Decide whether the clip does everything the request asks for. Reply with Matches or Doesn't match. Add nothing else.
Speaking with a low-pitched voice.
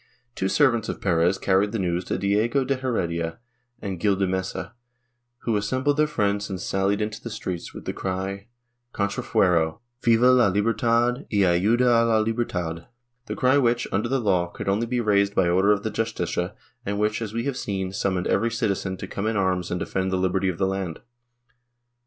Matches